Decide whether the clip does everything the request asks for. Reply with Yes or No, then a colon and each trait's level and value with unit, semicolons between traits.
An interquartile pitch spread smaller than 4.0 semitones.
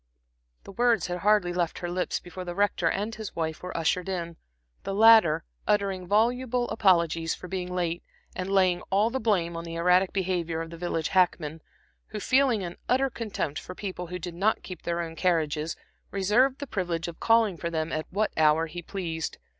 Yes: average, 3.6 semitones